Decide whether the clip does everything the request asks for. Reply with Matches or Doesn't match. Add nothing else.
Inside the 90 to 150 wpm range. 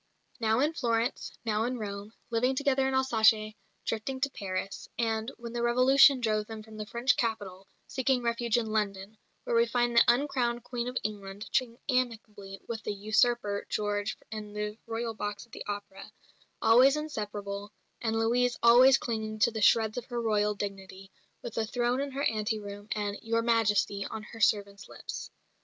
Doesn't match